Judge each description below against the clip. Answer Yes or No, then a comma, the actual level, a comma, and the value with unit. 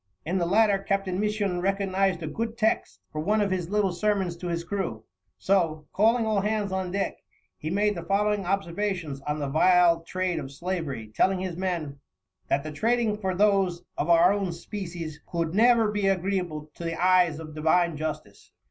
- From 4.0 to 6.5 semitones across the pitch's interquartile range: No, average, 3.2 semitones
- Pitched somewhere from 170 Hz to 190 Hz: Yes, medium, 185 Hz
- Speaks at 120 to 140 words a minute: No, average, 185 wpm